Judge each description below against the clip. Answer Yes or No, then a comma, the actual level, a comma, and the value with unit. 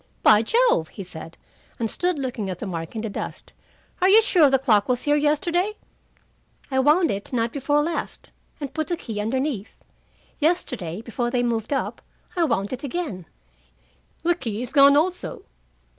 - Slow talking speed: No, average, 175 wpm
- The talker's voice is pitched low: No, very high, 265 Hz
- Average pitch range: No, wide, 6.1 semitones